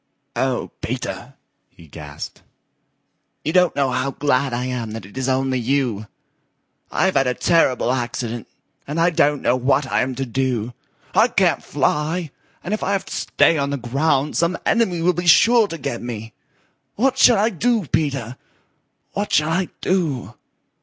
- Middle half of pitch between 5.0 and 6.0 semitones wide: Yes, wide, 5.4 semitones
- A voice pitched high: No, medium, 140 Hz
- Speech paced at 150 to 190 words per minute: Yes, average, 170 wpm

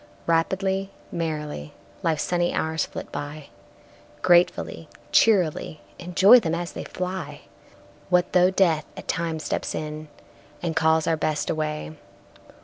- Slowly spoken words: Yes, slow, 125 wpm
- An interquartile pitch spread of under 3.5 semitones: Yes, narrow, 2.6 semitones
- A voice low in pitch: No, medium, 165 Hz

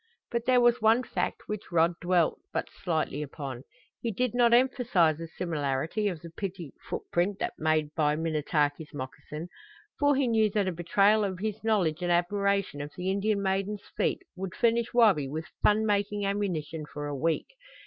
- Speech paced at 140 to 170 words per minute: No, average, 180 wpm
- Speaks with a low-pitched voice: No, medium, 185 Hz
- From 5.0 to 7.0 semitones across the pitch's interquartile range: Yes, average, 5.3 semitones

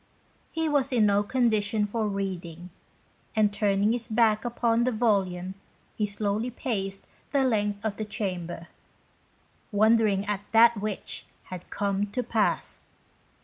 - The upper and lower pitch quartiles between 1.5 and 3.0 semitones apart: Yes, narrow, 2.5 semitones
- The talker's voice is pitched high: Yes, high, 210 Hz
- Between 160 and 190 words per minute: No, slow, 135 wpm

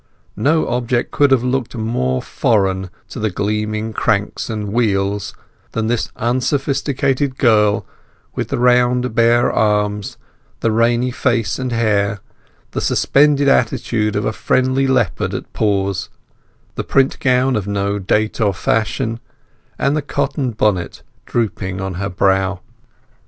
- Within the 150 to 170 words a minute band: No, slow, 135 wpm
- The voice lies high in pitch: No, low, 110 Hz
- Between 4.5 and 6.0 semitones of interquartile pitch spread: No, average, 3.8 semitones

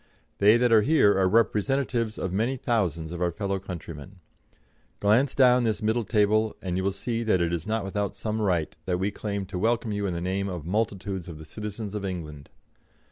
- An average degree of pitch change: Yes, average, 3.4 semitones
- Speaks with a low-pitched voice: Yes, low, 100 Hz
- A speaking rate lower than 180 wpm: No, fast, 205 wpm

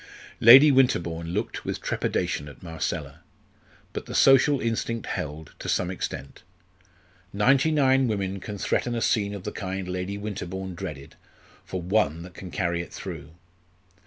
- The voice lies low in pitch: Yes, very low, 95 Hz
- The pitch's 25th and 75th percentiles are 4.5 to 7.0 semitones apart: Yes, average, 5.1 semitones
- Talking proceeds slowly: No, average, 150 wpm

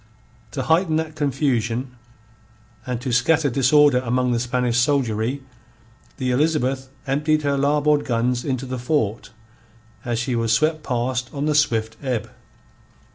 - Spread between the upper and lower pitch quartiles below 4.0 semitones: Yes, average, 3.3 semitones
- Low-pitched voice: Yes, low, 130 Hz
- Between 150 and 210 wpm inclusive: No, slow, 135 wpm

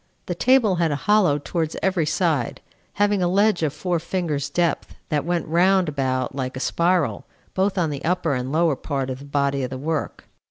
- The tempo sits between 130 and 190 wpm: No, average, 200 wpm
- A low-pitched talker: No, medium, 160 Hz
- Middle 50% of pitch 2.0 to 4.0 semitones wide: No, average, 4.4 semitones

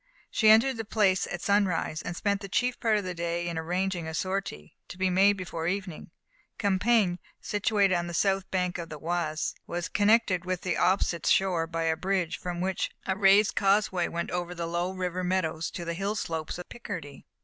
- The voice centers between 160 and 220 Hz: Yes, medium, 185 Hz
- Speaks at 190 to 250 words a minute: Yes, average, 200 wpm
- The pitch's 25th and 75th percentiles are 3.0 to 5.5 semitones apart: No, narrow, 2.5 semitones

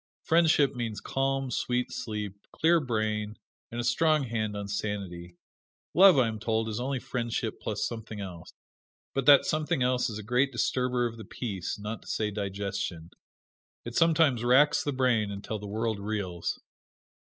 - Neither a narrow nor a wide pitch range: Yes, average, 3.8 semitones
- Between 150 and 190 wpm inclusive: Yes, average, 165 wpm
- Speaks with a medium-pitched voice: No, low, 115 Hz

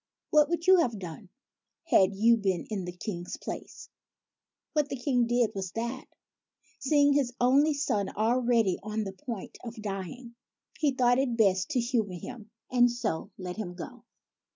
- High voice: Yes, high, 235 Hz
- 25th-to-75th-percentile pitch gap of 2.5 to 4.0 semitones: No, average, 4.8 semitones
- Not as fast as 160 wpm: No, average, 165 wpm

